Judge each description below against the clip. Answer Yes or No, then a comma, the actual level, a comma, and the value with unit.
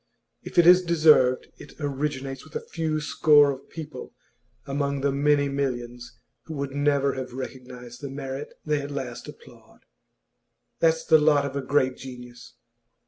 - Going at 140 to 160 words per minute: Yes, average, 155 wpm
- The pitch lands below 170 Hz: Yes, medium, 140 Hz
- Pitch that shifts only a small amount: Yes, narrow, 2.3 semitones